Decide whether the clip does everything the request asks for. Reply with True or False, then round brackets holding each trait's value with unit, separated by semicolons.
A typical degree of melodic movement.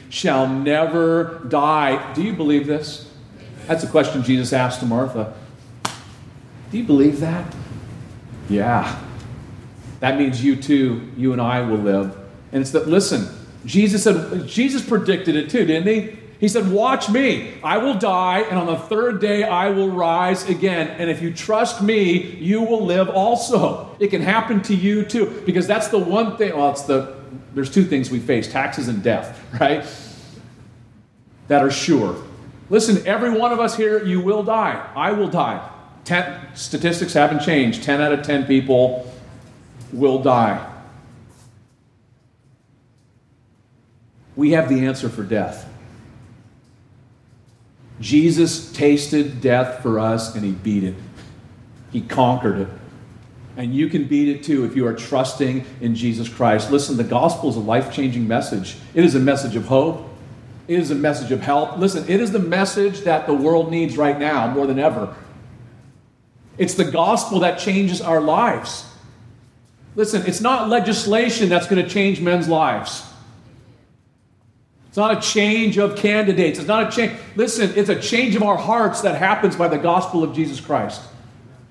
False (6.9 semitones)